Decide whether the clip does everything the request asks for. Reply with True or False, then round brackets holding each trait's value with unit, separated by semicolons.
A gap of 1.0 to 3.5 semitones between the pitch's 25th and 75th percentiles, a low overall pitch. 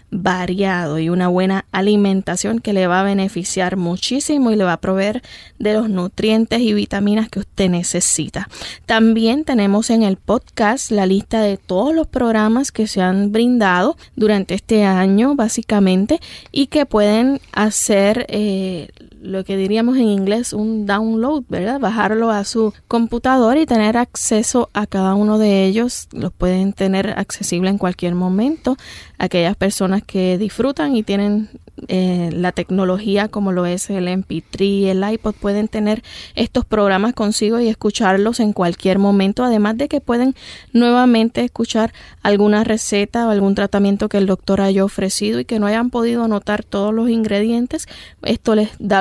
False (2.8 semitones; 210 Hz)